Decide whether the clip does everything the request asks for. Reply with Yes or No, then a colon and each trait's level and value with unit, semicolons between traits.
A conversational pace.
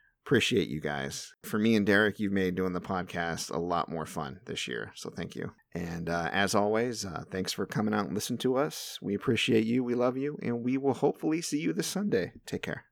No: fast, 230 wpm